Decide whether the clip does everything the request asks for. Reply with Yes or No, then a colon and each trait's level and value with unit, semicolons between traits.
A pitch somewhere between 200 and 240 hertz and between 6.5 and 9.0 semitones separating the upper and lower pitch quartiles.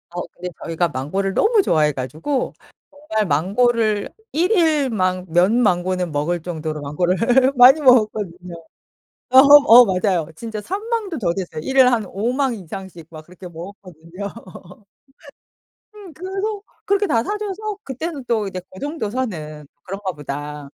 Yes: high, 205 Hz; wide, 7.7 semitones